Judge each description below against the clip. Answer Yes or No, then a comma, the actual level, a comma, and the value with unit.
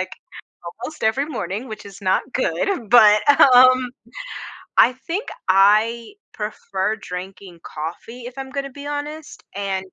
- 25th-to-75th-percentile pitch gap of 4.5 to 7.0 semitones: Yes, wide, 5.4 semitones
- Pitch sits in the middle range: No, high, 230 Hz